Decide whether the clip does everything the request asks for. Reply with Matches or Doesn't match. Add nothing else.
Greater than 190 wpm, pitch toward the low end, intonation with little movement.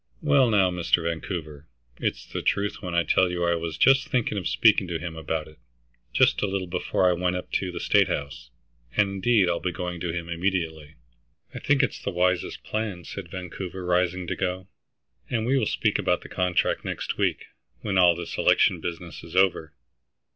Matches